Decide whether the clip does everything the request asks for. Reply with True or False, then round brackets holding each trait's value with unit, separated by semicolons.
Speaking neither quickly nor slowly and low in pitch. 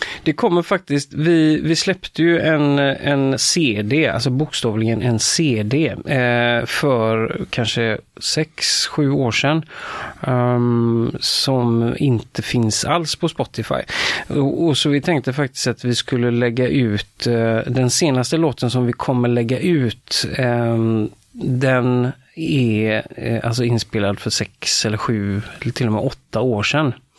True (140 wpm; 125 Hz)